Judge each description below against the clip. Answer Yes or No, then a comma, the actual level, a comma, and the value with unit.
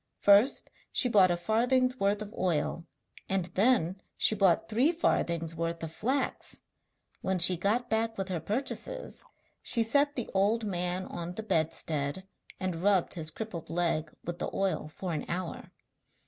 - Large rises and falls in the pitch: No, average, 4.7 semitones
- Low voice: No, high, 190 Hz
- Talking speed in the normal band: Yes, average, 160 wpm